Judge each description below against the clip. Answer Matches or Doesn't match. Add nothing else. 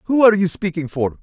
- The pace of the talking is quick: Matches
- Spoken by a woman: Doesn't match